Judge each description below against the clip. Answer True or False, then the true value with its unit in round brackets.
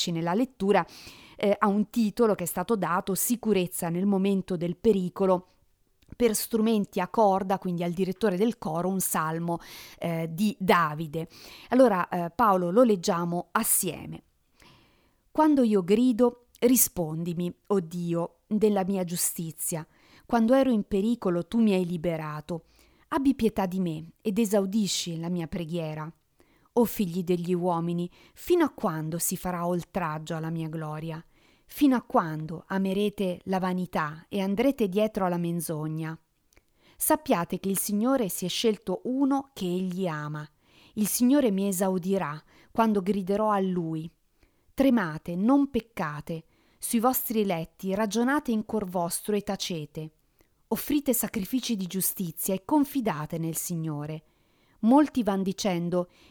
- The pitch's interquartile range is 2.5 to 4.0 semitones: False (4.4 semitones)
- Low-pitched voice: False (190 Hz)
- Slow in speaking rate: False (135 wpm)